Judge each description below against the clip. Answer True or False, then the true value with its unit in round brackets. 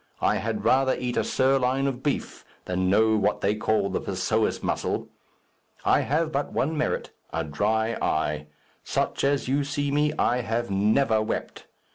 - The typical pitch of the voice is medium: False (120 Hz)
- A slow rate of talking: False (165 wpm)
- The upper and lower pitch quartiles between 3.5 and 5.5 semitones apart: True (5.0 semitones)